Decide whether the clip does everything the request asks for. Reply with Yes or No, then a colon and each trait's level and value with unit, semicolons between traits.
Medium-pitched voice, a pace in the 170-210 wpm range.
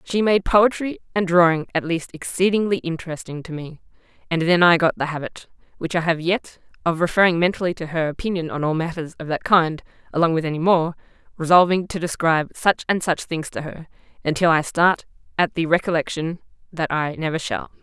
Yes: medium, 170 Hz; average, 190 wpm